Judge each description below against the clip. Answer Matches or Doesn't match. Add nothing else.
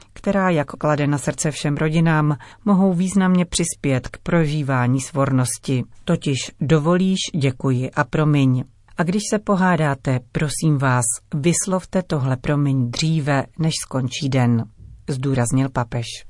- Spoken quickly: Doesn't match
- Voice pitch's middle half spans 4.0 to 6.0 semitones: Matches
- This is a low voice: Doesn't match